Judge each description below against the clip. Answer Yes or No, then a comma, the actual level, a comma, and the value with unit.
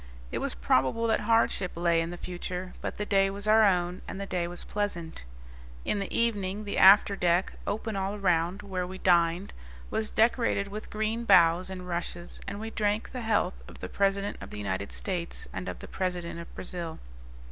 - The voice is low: No, high, 190 Hz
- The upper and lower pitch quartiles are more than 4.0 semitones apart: No, average, 3.0 semitones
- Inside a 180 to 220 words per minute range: Yes, average, 195 wpm